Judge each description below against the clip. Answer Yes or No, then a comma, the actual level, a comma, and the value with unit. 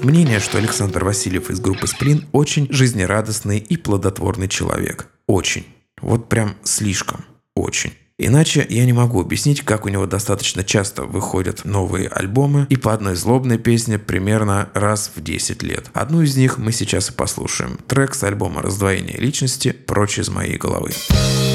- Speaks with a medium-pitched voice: No, low, 105 Hz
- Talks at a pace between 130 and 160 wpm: Yes, average, 155 wpm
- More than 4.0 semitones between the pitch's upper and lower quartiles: Yes, average, 4.6 semitones